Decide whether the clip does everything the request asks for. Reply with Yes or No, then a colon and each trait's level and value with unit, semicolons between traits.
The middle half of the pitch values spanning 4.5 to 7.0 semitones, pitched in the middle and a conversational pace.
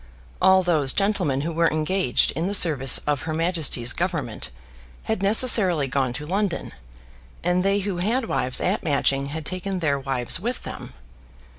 Yes: average, 5.3 semitones; medium, 170 Hz; average, 160 wpm